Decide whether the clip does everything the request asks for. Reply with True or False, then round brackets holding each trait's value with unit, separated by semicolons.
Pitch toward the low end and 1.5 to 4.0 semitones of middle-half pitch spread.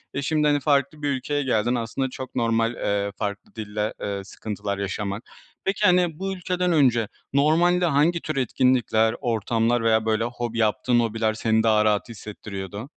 False (120 Hz; 5.0 semitones)